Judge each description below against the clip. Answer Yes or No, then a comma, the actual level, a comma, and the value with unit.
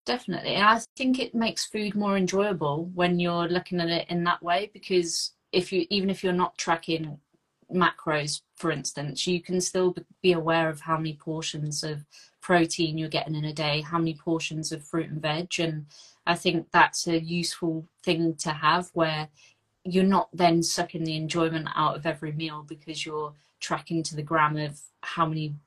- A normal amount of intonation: No, narrow, 2.3 semitones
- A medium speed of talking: Yes, average, 185 wpm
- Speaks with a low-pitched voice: No, medium, 165 Hz